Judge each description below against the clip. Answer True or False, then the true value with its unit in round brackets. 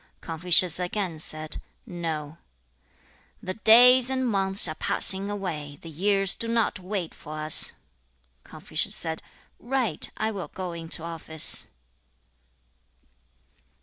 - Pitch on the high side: False (180 Hz)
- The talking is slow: True (115 wpm)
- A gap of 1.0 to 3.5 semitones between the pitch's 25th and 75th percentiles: False (4.3 semitones)